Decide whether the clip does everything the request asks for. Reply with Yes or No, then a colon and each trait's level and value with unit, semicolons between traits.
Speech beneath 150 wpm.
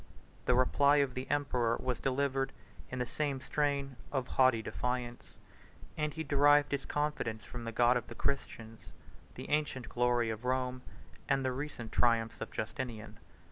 No: average, 160 wpm